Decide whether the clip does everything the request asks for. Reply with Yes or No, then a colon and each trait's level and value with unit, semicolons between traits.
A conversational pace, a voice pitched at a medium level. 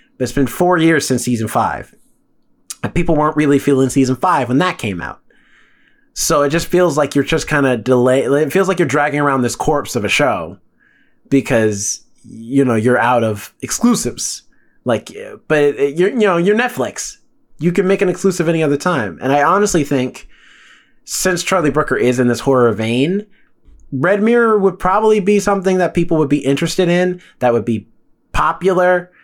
Yes: average, 185 wpm; medium, 155 Hz